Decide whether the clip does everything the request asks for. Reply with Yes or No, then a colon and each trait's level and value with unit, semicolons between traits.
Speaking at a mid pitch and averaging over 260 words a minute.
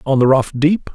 No: medium, 145 Hz; fast, 255 wpm